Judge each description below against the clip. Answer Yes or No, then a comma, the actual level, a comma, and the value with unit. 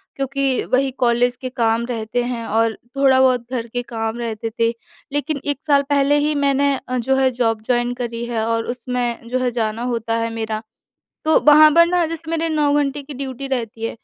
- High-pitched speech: Yes, very high, 250 Hz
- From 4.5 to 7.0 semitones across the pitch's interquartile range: No, average, 3.3 semitones